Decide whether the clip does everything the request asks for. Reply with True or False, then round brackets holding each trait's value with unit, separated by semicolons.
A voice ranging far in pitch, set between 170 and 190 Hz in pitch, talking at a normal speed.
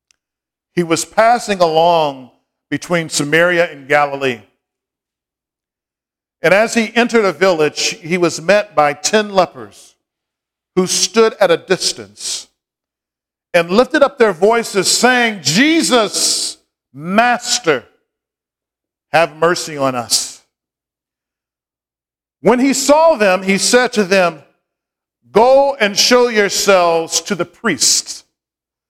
False (6.1 semitones; 185 Hz; 110 wpm)